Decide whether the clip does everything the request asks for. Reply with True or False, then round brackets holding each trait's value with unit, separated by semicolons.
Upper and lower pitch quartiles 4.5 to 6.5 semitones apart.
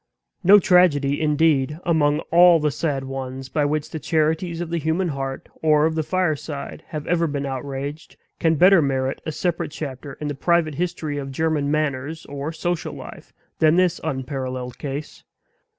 False (2.9 semitones)